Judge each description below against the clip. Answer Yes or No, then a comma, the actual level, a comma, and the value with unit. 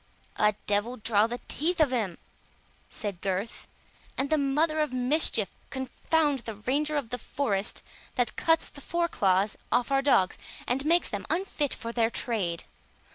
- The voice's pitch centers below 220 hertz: No, very high, 250 Hz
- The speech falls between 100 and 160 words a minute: Yes, average, 155 wpm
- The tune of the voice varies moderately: No, wide, 5.9 semitones